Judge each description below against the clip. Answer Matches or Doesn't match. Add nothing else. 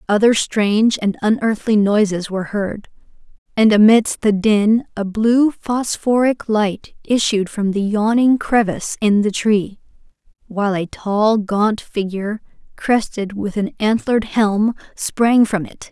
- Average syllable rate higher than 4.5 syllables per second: Doesn't match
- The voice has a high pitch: Matches